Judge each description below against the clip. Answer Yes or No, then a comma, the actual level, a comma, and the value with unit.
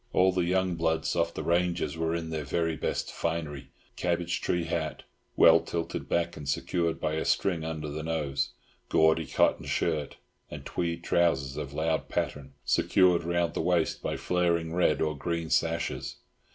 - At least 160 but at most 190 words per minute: Yes, average, 165 wpm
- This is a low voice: Yes, very low, 80 Hz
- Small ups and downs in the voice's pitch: Yes, narrow, 1.7 semitones